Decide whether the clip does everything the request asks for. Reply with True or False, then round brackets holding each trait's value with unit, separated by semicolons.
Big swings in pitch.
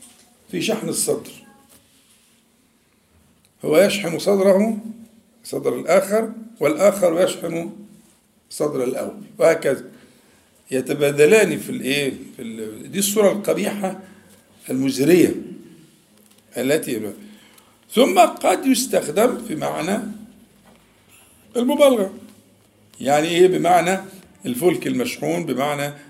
True (6.3 semitones)